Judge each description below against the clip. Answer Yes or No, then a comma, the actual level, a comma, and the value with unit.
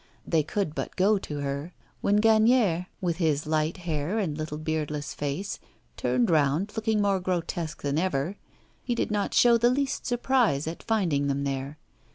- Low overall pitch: No, medium, 165 Hz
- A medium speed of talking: Yes, average, 170 wpm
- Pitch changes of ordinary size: No, wide, 6.0 semitones